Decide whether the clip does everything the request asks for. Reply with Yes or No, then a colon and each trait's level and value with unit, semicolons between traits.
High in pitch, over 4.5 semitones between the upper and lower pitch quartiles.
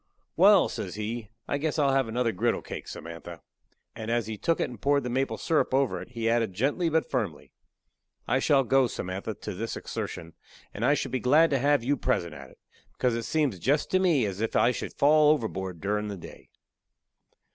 No: low, 120 Hz; average, 5.3 semitones